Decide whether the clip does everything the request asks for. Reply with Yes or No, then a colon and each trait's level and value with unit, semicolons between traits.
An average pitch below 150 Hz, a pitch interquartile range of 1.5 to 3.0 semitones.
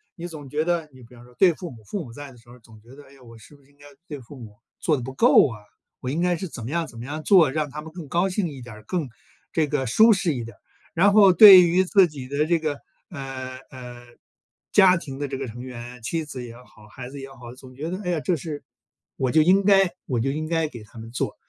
No: medium, 140 Hz; average, 5.2 semitones